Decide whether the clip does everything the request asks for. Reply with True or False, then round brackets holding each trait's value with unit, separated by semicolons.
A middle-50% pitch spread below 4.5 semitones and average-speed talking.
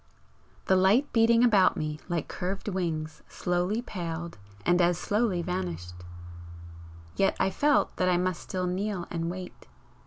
True (2.4 semitones; 145 wpm)